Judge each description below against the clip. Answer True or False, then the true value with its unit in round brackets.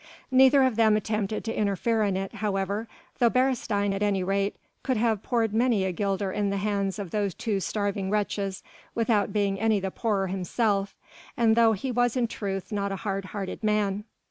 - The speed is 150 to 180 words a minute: False (190 wpm)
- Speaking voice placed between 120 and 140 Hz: False (205 Hz)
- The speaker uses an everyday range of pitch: False (2.3 semitones)